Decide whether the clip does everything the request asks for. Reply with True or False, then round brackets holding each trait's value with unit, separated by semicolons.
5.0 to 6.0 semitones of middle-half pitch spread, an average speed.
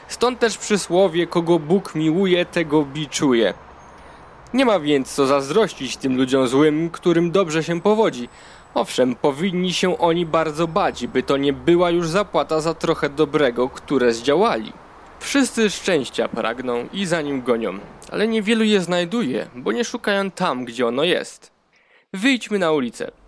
True (5.6 semitones; 150 wpm)